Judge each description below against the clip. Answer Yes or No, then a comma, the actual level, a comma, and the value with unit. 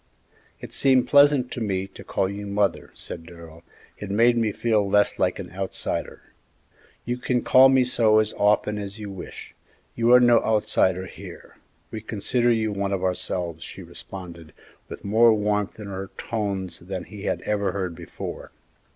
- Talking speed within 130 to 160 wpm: No, average, 170 wpm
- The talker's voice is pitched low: Yes, low, 105 Hz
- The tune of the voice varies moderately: Yes, average, 3.4 semitones